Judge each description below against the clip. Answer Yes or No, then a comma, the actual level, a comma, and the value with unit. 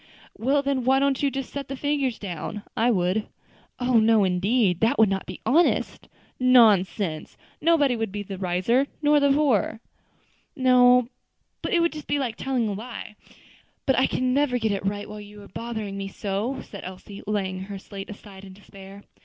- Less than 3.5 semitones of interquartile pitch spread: No, average, 4.9 semitones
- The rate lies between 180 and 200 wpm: Yes, average, 190 wpm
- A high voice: Yes, high, 225 Hz